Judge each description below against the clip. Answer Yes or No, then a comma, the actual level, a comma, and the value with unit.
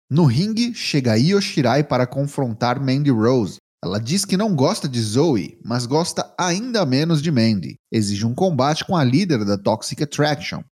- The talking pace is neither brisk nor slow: Yes, average, 165 wpm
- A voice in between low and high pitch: Yes, medium, 145 Hz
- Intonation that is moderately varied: No, wide, 6.6 semitones